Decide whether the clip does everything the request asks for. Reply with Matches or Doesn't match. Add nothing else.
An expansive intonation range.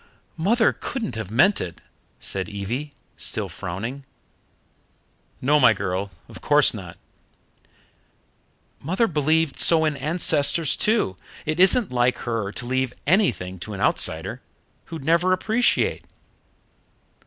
Matches